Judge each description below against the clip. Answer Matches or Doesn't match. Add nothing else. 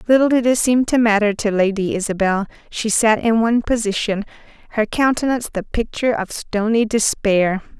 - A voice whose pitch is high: Matches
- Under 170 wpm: Matches